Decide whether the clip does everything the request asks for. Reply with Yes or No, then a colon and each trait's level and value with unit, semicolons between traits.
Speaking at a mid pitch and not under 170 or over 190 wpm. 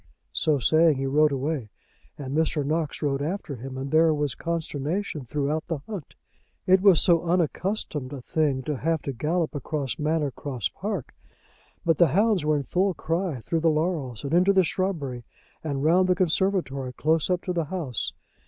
Yes: medium, 155 Hz; average, 180 wpm